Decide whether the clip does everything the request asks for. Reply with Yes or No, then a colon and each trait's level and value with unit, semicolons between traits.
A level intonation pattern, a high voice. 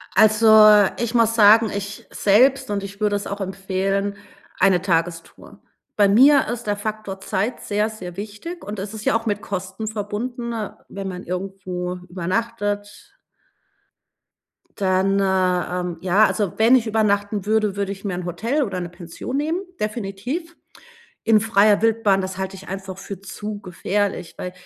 Yes: narrow, 2.3 semitones; high, 205 Hz